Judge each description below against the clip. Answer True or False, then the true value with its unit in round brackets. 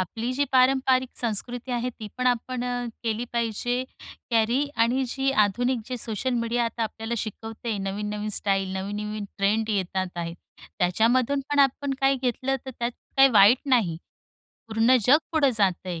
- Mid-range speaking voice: False (230 Hz)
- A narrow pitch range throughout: False (3.5 semitones)